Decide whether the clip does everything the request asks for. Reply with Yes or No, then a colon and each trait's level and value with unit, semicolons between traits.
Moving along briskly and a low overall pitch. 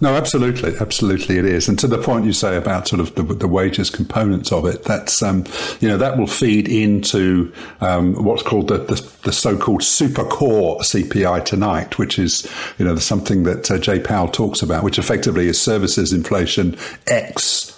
No: average, 190 wpm; low, 100 Hz